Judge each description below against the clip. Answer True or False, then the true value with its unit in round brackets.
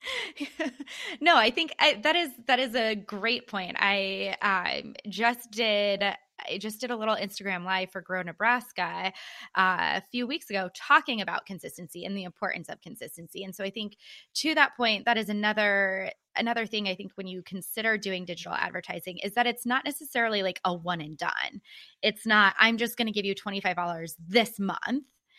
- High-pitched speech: True (210 Hz)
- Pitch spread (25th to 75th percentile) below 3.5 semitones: False (4.2 semitones)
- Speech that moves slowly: False (185 wpm)